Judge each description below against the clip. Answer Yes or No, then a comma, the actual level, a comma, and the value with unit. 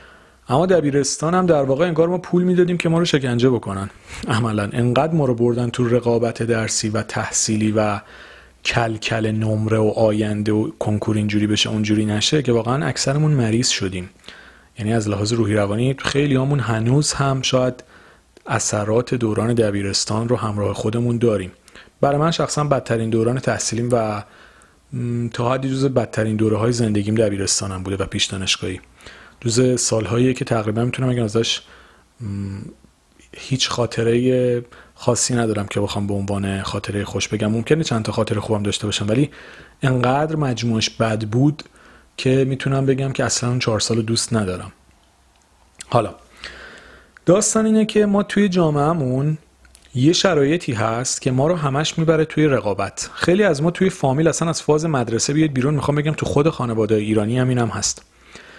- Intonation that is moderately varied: Yes, average, 4.2 semitones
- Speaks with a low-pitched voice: Yes, low, 120 Hz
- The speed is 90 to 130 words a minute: No, fast, 155 wpm